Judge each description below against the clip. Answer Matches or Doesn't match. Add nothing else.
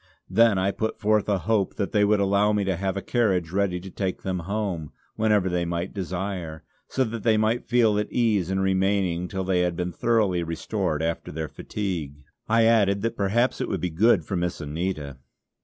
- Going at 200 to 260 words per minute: Matches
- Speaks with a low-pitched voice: Matches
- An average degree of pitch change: Matches